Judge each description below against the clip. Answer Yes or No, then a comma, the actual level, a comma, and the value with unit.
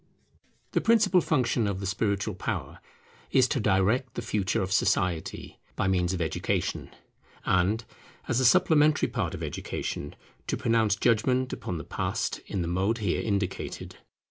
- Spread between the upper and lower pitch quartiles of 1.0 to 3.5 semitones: No, average, 5.1 semitones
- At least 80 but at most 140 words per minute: No, average, 150 wpm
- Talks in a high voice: No, low, 105 Hz